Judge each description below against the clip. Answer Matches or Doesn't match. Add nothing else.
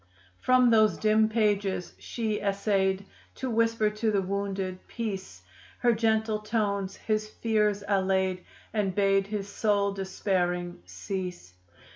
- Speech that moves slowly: Matches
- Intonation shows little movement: Matches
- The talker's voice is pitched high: Matches